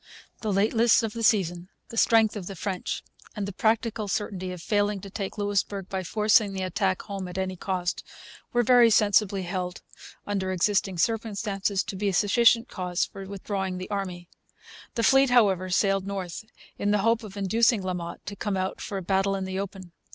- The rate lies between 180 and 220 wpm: Yes, average, 190 wpm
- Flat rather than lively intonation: Yes, narrow, 2.2 semitones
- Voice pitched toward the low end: No, high, 195 Hz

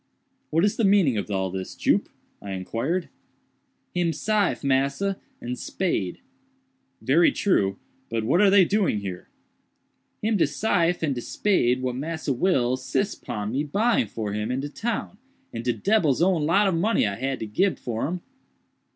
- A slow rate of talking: No, average, 170 wpm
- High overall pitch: No, medium, 145 Hz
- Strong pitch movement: Yes, wide, 8.5 semitones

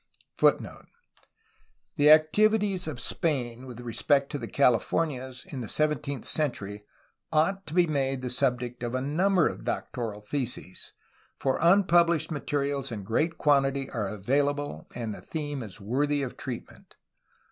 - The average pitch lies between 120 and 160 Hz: Yes, medium, 140 Hz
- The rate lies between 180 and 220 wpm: No, average, 150 wpm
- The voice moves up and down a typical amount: Yes, average, 4.0 semitones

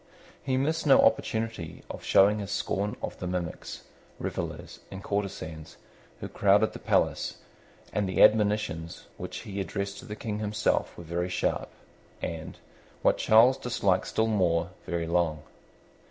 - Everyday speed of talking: Yes, average, 145 wpm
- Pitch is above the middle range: No, low, 100 Hz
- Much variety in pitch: No, average, 3.9 semitones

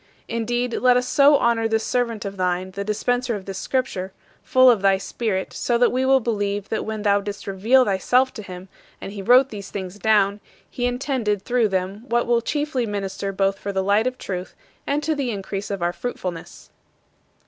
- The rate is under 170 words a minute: No, average, 200 wpm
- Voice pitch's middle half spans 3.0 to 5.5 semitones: Yes, average, 4.1 semitones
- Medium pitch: No, high, 215 Hz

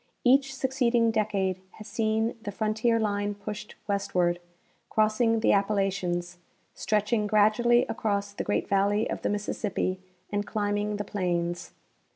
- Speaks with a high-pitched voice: Yes, high, 210 Hz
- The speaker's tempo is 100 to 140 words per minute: Yes, slow, 135 wpm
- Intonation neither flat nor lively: No, narrow, 1.8 semitones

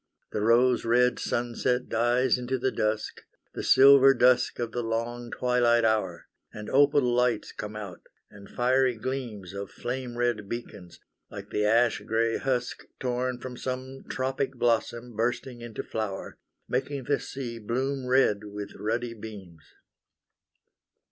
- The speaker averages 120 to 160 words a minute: Yes, average, 140 wpm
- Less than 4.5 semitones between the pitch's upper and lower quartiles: Yes, narrow, 2.6 semitones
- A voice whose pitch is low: Yes, low, 120 Hz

